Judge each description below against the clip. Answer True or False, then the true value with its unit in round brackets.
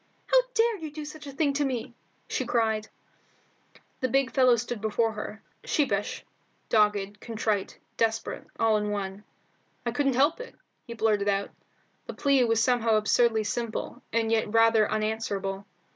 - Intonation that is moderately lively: True (3.3 semitones)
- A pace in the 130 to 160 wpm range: True (155 wpm)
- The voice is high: True (225 Hz)